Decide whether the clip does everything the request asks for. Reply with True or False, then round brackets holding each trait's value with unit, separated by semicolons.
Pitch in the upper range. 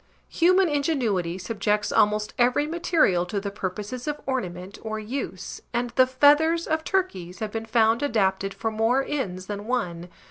True (225 Hz)